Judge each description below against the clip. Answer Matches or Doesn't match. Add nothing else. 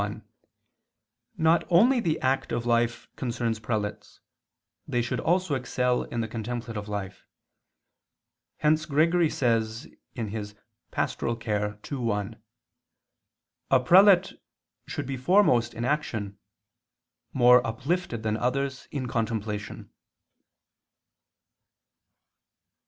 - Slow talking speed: Matches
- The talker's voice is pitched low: Matches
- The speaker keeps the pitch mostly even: Doesn't match